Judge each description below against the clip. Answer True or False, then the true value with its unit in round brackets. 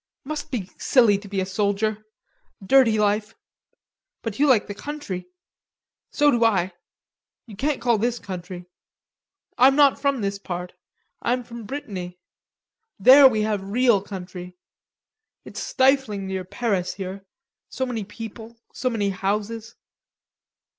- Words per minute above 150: False (135 wpm)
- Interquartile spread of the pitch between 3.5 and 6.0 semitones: True (4.2 semitones)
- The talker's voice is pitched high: True (215 Hz)